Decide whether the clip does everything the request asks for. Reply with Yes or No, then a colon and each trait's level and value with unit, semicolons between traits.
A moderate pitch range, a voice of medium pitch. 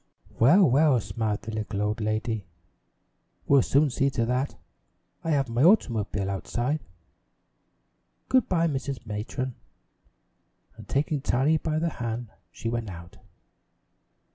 No: average, 4.9 semitones; low, 120 Hz